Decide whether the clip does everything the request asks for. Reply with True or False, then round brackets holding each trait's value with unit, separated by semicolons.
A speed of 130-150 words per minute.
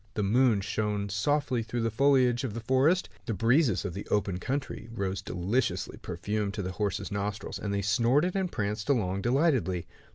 False (175 wpm)